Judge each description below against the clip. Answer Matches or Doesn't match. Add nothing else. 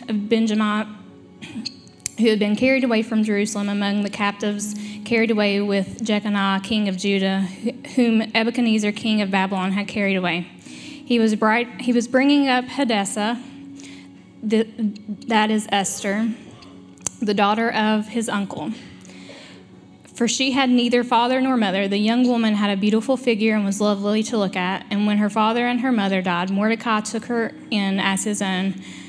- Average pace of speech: Matches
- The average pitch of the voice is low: Doesn't match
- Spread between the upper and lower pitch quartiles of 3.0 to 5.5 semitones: Doesn't match